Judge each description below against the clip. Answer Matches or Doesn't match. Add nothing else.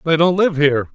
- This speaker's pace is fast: Matches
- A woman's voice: Doesn't match